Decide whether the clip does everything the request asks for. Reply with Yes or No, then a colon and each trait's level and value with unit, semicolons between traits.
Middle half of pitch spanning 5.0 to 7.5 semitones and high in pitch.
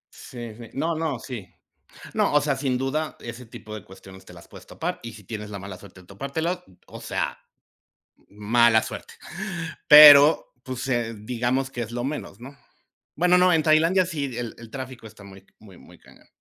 No: average, 5.3 semitones; low, 120 Hz